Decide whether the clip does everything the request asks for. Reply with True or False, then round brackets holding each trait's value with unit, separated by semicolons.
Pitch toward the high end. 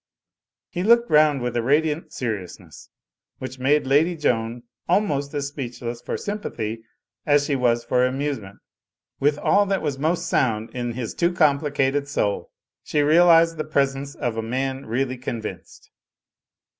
False (140 Hz)